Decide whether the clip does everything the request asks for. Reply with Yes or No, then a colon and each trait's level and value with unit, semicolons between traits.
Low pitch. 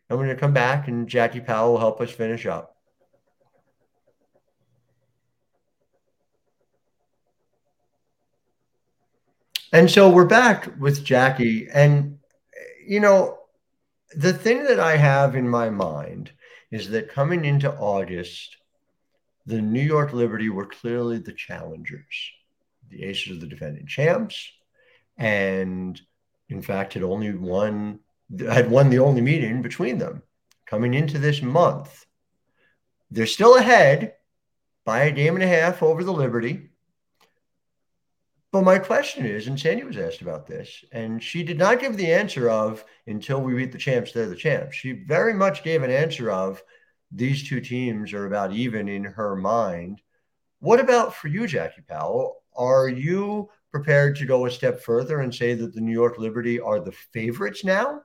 Yes: low, 130 Hz